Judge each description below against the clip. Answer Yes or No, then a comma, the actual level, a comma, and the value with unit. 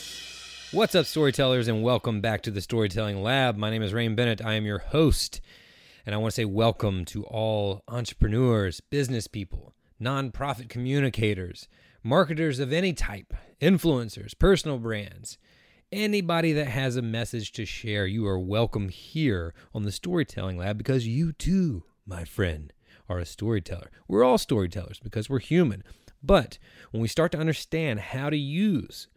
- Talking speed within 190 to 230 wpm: No, average, 160 wpm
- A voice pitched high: No, low, 115 Hz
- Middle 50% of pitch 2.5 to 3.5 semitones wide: No, average, 5.3 semitones